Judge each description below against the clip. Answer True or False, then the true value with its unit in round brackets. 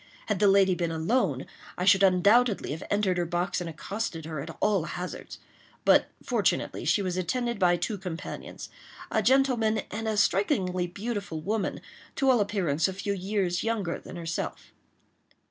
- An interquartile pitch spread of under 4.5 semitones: True (3.5 semitones)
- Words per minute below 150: False (160 wpm)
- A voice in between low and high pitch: False (195 Hz)